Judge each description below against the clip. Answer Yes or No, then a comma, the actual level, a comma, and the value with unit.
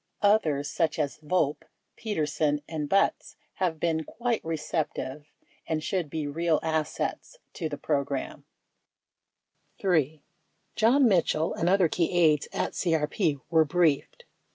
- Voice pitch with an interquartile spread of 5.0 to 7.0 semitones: No, average, 2.9 semitones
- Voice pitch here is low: No, medium, 160 Hz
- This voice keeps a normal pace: No, slow, 125 wpm